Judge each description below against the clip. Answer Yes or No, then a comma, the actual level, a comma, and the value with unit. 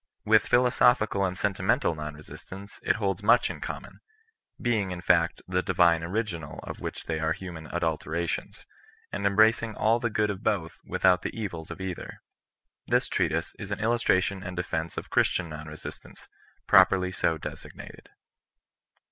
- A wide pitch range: No, average, 4.2 semitones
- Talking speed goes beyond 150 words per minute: Yes, average, 160 wpm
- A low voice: Yes, very low, 95 Hz